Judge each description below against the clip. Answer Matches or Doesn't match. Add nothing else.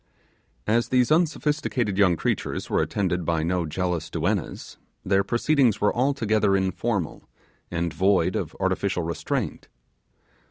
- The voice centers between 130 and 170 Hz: Doesn't match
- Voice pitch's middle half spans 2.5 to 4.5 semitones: Doesn't match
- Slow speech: Matches